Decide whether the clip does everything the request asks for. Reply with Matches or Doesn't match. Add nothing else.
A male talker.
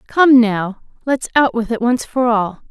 Doesn't match